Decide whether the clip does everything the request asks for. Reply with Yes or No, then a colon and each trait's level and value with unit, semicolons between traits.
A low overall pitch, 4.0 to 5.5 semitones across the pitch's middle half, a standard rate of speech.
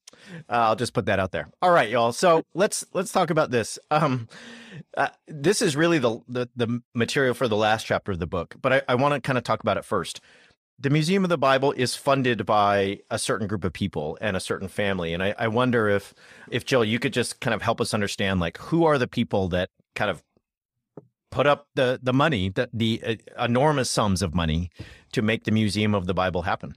No: low, 120 Hz; average, 5.1 semitones; fast, 230 wpm